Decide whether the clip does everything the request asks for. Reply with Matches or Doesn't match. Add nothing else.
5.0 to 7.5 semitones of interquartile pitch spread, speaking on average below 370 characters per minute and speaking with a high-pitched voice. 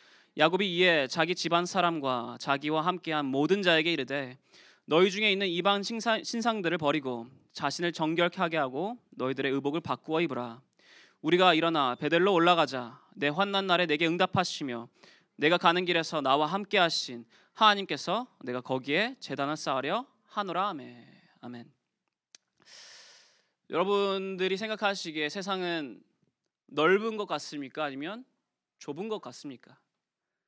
Doesn't match